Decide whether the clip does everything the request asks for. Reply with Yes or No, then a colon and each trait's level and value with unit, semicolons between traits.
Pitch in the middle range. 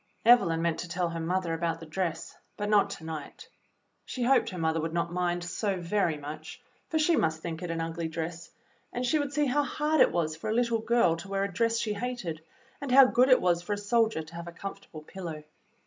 Yes: medium, 180 Hz